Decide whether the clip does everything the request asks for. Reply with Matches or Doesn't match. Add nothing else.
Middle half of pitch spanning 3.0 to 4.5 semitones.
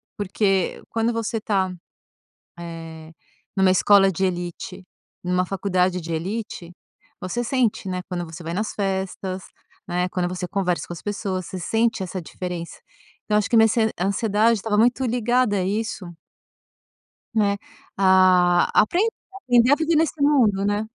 Matches